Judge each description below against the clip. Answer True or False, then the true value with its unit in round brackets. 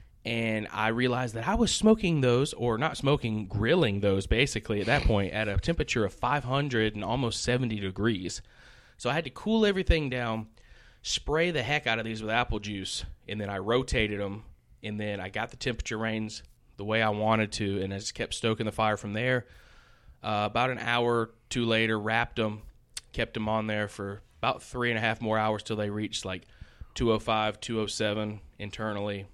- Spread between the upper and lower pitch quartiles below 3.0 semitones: True (2.5 semitones)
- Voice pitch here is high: False (110 Hz)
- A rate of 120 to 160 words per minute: False (195 wpm)